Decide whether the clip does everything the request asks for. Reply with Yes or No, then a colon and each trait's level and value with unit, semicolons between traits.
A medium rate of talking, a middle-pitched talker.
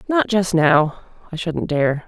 Yes: average, 145 wpm; medium, 175 Hz